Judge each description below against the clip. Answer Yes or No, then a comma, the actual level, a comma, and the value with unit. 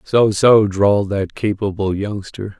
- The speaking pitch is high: No, low, 100 Hz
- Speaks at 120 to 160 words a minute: Yes, average, 140 wpm